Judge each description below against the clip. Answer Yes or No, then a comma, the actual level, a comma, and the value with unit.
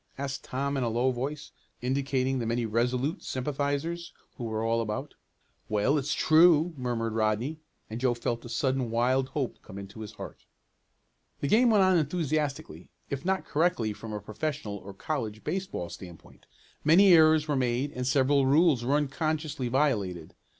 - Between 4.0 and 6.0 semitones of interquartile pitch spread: Yes, average, 4.6 semitones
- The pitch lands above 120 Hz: Yes, low, 135 Hz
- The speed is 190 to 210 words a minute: No, average, 165 wpm